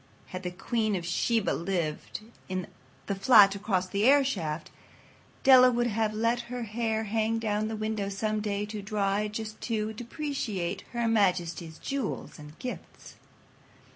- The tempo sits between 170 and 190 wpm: No, average, 145 wpm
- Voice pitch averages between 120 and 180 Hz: No, high, 215 Hz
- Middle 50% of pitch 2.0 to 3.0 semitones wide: Yes, average, 2.7 semitones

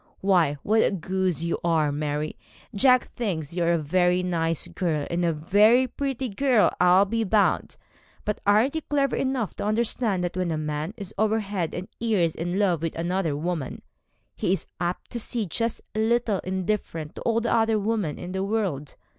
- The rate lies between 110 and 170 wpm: No, average, 190 wpm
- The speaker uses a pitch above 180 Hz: Yes, high, 190 Hz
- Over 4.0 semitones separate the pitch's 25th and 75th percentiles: Yes, average, 4.8 semitones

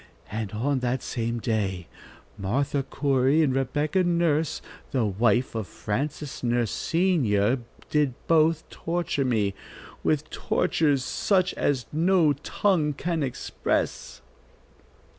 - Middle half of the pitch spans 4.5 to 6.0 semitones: Yes, average, 5.0 semitones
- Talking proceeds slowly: Yes, slow, 110 wpm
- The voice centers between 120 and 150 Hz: Yes, low, 135 Hz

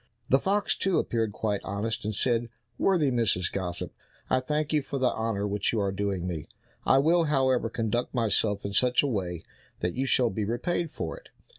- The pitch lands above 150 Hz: No, low, 115 Hz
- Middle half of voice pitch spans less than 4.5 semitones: No, average, 5.0 semitones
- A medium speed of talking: Yes, average, 195 wpm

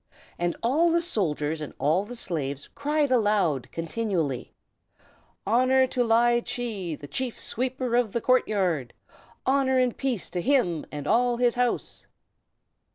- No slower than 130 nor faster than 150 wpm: Yes, average, 145 wpm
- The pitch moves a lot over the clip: Yes, wide, 7.0 semitones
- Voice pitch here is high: Yes, high, 230 Hz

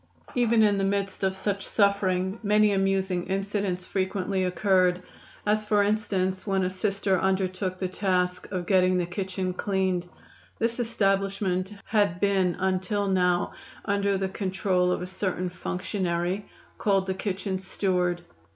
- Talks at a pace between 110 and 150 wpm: Yes, average, 140 wpm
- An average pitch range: No, narrow, 1.6 semitones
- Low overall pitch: No, high, 190 Hz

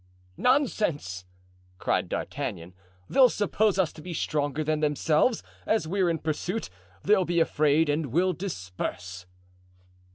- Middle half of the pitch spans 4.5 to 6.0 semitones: Yes, average, 4.8 semitones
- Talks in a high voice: No, medium, 160 Hz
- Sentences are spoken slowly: Yes, slow, 125 wpm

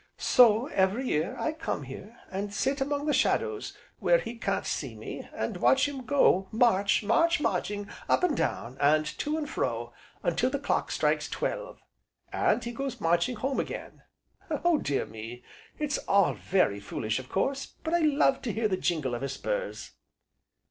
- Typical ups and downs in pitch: No, wide, 8.8 semitones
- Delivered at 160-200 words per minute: Yes, average, 175 wpm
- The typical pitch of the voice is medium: No, high, 230 Hz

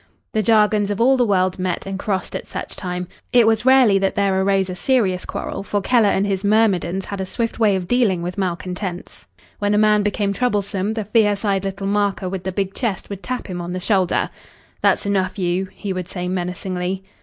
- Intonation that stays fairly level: Yes, narrow, 2.2 semitones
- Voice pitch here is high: Yes, high, 195 Hz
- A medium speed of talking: No, fast, 210 wpm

